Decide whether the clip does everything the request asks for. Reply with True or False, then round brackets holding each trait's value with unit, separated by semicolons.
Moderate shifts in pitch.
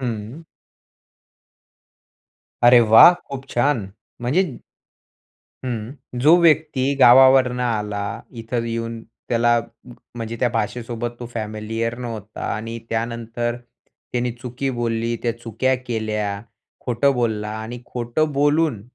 False (2.2 semitones)